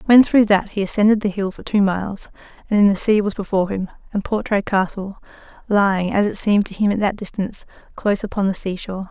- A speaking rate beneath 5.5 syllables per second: No, 6.3 syllables/s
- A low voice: No, high, 200 Hz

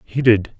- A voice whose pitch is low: Yes, low, 115 Hz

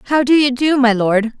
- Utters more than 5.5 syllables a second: No, 5.2 syllables/s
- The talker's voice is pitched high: Yes, very high, 255 Hz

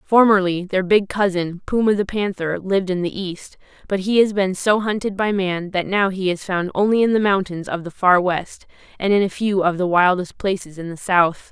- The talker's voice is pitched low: No, high, 190 Hz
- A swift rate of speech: Yes, fast, 225 wpm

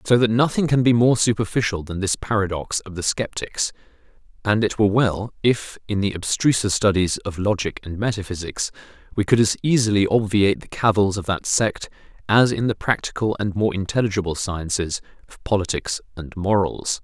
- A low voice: Yes, low, 105 Hz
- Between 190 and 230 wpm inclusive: No, average, 170 wpm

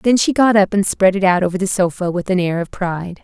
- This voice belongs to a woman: Yes, female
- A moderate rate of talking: No, fast, 295 wpm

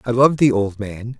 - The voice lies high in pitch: No, low, 115 Hz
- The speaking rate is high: Yes, fast, 250 wpm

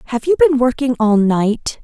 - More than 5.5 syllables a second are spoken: No, 4.5 syllables/s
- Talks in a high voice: Yes, very high, 250 Hz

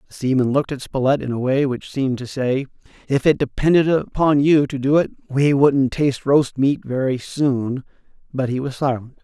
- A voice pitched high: No, low, 135 Hz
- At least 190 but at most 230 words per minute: Yes, average, 200 wpm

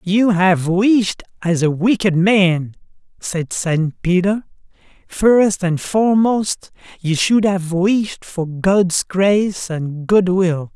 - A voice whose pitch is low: No, medium, 185 Hz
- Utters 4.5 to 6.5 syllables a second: No, 3.1 syllables/s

